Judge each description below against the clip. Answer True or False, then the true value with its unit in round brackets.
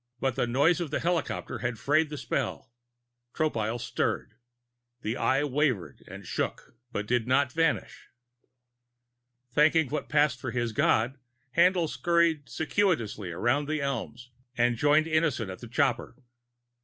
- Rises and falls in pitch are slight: False (4.6 semitones)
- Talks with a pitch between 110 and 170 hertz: True (140 Hz)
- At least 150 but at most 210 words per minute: False (140 wpm)